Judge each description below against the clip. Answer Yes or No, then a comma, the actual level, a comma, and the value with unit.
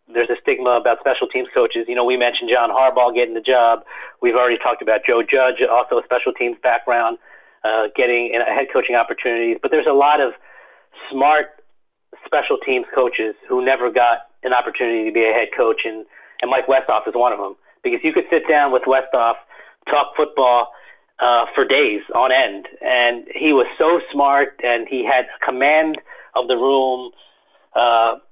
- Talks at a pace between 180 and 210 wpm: Yes, average, 185 wpm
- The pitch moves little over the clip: No, average, 3.1 semitones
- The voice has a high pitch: No, low, 125 Hz